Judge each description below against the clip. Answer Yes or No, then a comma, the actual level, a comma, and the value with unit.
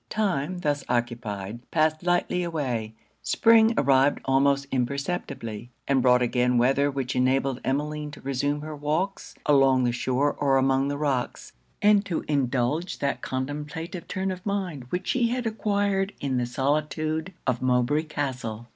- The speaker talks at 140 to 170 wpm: Yes, average, 145 wpm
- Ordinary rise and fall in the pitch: Yes, average, 4.3 semitones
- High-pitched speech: No, medium, 140 Hz